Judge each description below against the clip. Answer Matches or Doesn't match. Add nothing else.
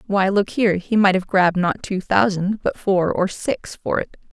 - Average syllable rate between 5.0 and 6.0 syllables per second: Doesn't match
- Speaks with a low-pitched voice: Doesn't match